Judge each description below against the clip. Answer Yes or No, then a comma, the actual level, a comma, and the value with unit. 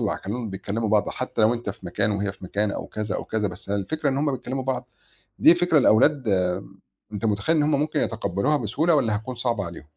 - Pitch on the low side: Yes, low, 110 Hz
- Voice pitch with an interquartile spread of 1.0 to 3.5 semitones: No, average, 4.8 semitones